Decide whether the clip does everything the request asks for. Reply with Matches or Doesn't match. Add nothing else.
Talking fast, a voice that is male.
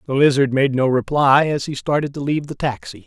Matches